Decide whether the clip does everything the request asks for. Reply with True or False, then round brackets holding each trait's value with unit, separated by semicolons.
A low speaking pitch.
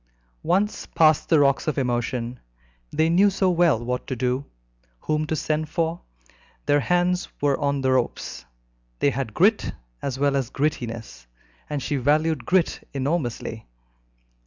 False (145 Hz)